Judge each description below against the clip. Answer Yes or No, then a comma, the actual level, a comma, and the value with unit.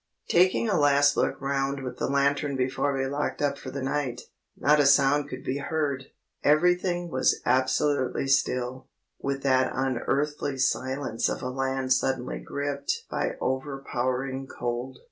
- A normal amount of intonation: No, narrow, 1.7 semitones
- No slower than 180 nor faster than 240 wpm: No, average, 145 wpm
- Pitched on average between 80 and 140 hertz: Yes, low, 135 Hz